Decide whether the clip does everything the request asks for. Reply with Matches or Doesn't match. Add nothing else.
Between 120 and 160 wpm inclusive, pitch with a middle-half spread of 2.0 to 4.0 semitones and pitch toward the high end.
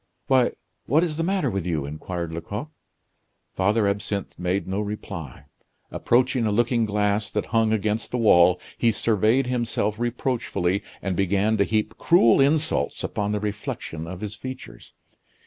Doesn't match